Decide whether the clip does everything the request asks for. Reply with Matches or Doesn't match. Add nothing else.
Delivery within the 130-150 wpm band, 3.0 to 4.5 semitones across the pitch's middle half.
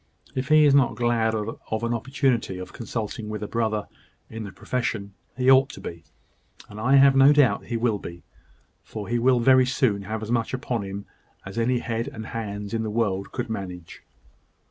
Doesn't match